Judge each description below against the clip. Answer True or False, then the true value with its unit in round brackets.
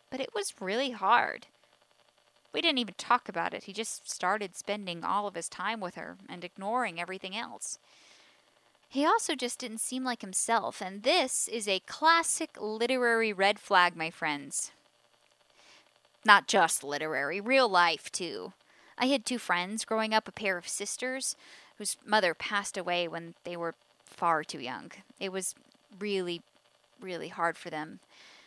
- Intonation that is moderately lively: False (5.8 semitones)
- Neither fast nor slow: True (160 wpm)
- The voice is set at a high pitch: True (210 Hz)